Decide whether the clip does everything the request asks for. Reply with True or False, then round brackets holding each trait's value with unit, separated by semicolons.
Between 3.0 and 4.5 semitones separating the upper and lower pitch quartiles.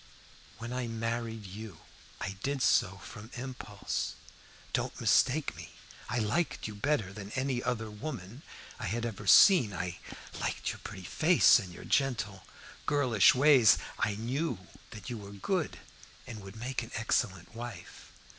True (4.0 semitones)